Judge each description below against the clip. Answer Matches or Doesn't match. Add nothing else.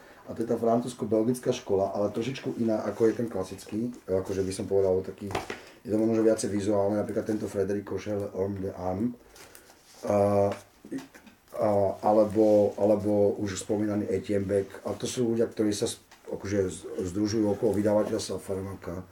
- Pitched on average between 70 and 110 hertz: Matches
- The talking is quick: Doesn't match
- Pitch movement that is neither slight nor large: Doesn't match